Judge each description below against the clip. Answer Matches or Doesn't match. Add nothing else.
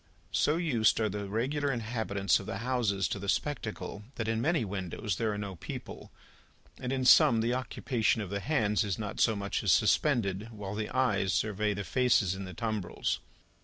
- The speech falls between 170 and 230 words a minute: Matches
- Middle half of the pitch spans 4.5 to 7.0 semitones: Doesn't match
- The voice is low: Matches